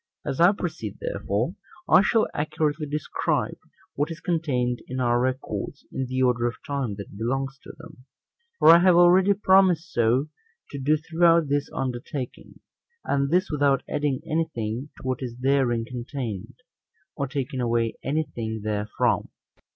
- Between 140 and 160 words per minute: Yes, average, 155 wpm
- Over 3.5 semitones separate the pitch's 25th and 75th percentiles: Yes, average, 4.5 semitones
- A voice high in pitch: No, medium, 140 Hz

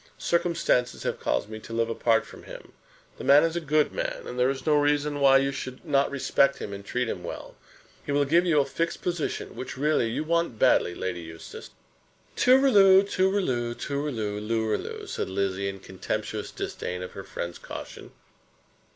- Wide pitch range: Yes, wide, 5.9 semitones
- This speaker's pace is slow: No, average, 180 wpm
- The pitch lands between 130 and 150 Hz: Yes, low, 135 Hz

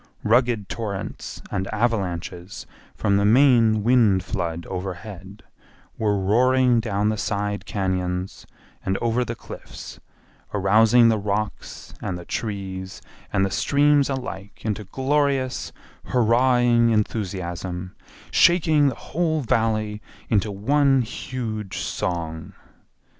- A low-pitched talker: Yes, low, 110 Hz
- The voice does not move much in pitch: No, average, 4.1 semitones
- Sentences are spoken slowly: Yes, slow, 110 wpm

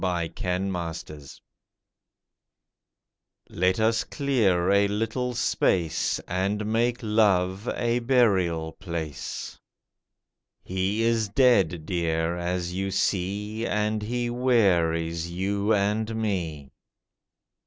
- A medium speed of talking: No, slow, 90 wpm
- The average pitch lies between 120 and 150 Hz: No, low, 100 Hz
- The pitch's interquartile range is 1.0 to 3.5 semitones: No, average, 4.2 semitones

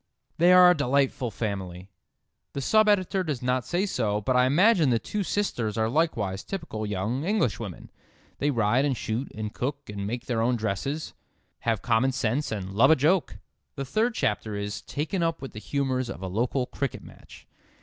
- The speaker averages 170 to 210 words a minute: Yes, average, 185 wpm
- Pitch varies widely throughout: Yes, wide, 5.9 semitones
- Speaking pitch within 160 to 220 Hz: No, low, 125 Hz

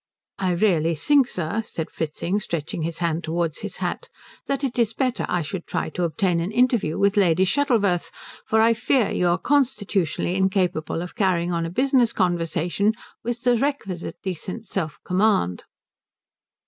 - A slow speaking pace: No, average, 160 wpm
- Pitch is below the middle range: No, high, 190 Hz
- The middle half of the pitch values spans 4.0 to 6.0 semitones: Yes, average, 5.2 semitones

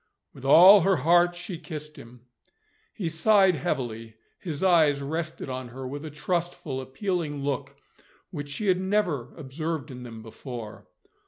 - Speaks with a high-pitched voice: No, medium, 150 Hz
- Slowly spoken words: No, average, 150 wpm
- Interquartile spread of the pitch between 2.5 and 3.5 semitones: No, average, 4.9 semitones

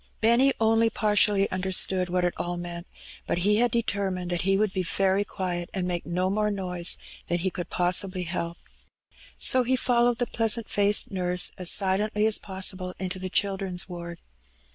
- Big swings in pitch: No, average, 2.8 semitones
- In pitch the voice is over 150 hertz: Yes, high, 190 Hz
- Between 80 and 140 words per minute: No, average, 175 wpm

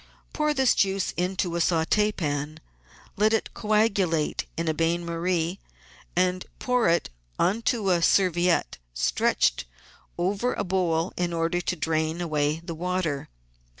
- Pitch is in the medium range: Yes, medium, 175 Hz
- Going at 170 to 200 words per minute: No, average, 140 wpm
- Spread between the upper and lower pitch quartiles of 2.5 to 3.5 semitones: Yes, average, 3.0 semitones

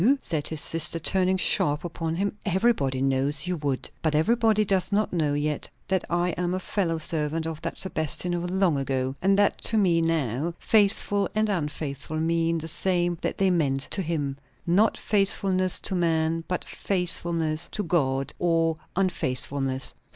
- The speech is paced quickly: No, average, 165 wpm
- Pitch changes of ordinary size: Yes, average, 3.7 semitones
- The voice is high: No, medium, 170 Hz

